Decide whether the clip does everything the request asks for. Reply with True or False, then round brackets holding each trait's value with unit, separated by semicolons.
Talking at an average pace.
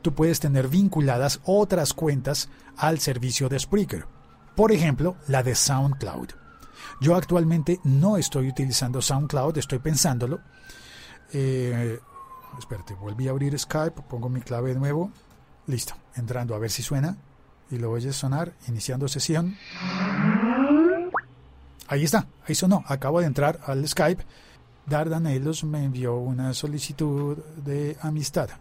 True (135 wpm)